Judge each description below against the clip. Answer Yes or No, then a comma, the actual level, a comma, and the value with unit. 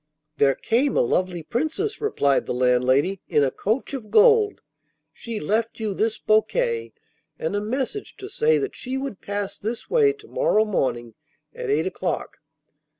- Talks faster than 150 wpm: Yes, average, 160 wpm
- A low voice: No, high, 225 Hz